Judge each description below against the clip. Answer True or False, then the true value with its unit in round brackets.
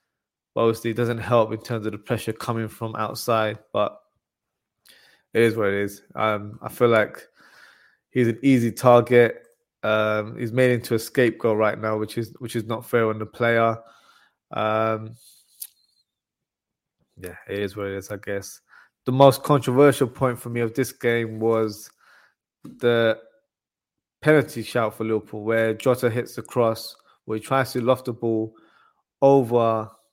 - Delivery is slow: False (160 wpm)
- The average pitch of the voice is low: True (115 Hz)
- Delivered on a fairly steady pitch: True (1.9 semitones)